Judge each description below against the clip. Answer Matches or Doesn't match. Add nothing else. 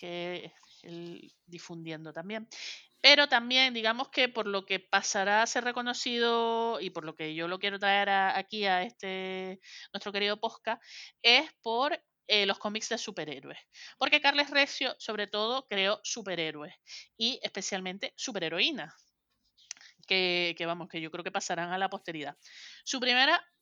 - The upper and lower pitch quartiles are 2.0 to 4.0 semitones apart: Doesn't match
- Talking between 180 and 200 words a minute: Doesn't match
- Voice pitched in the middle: Doesn't match